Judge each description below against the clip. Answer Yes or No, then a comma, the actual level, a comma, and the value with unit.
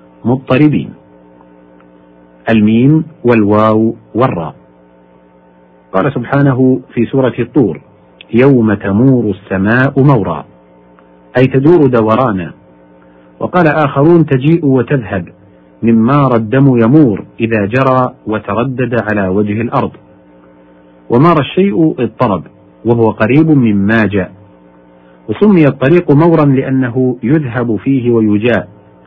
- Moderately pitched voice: No, low, 115 Hz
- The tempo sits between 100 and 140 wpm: No, average, 90 wpm